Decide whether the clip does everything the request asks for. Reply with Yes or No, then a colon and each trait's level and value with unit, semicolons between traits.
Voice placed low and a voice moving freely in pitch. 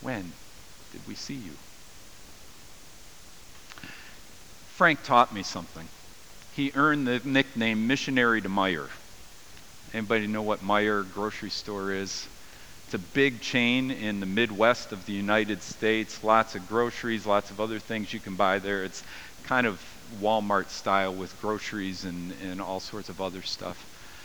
No: low, 105 Hz; average, 2.8 semitones